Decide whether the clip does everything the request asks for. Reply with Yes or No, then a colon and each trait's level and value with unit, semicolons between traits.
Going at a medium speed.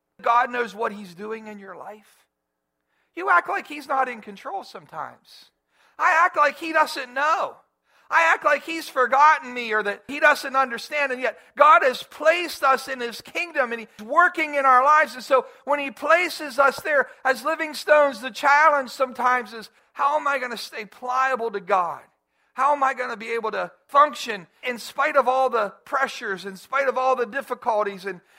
Yes: average, 195 wpm